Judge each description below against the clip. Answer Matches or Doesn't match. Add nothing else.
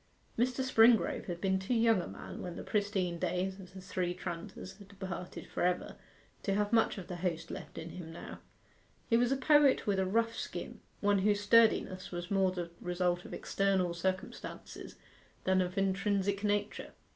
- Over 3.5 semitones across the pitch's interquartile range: Doesn't match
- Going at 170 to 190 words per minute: Matches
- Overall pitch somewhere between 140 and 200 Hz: Matches